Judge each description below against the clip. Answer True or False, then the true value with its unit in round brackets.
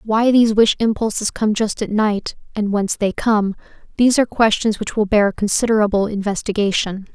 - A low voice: False (210 Hz)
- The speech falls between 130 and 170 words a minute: True (160 wpm)